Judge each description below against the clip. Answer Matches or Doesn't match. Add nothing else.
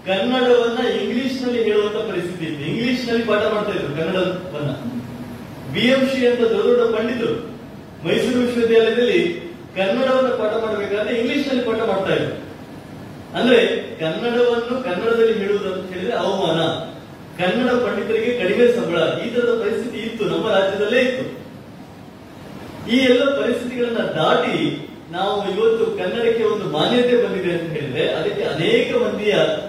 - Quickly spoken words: Matches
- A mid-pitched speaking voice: Doesn't match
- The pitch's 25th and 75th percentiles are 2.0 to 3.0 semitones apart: Doesn't match